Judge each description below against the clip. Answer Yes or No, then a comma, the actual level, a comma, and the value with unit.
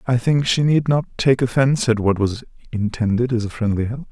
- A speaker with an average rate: No, fast, 220 wpm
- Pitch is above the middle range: No, low, 120 Hz